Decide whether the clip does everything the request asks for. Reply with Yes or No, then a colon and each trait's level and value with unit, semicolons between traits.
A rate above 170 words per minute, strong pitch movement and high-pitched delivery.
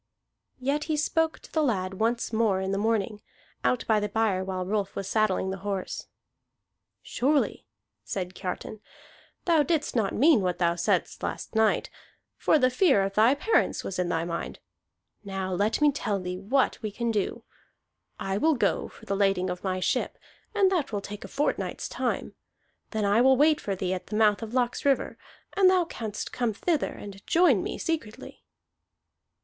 Yes: average, 180 wpm; wide, 5.8 semitones; high, 215 Hz